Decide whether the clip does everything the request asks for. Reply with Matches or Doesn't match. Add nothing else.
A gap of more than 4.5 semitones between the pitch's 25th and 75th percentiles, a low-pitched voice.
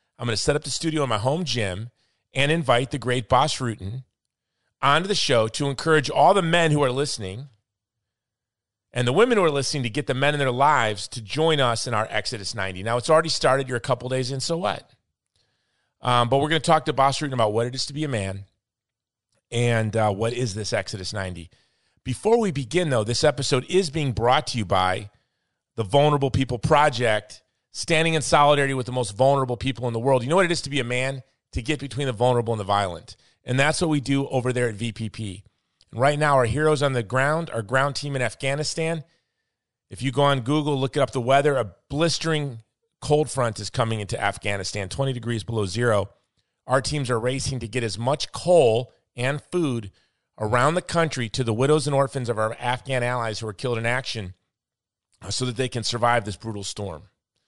Doesn't match